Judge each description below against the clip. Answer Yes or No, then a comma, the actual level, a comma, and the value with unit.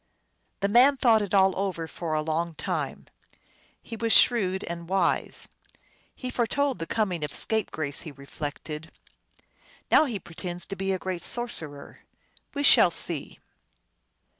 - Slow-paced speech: No, average, 155 wpm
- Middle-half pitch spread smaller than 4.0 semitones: No, wide, 5.6 semitones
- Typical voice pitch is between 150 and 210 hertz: Yes, high, 190 Hz